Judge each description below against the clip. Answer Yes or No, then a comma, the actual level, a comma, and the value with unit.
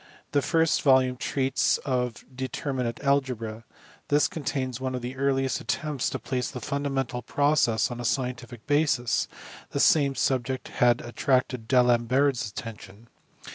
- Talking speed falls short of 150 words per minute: Yes, average, 140 wpm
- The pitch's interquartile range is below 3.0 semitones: Yes, narrow, 2.4 semitones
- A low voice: Yes, low, 130 Hz